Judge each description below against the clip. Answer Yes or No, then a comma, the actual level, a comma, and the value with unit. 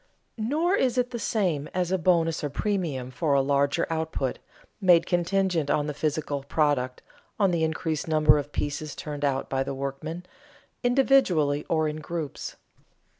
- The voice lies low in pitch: No, medium, 155 Hz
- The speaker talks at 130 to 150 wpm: No, average, 160 wpm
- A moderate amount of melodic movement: Yes, average, 4.0 semitones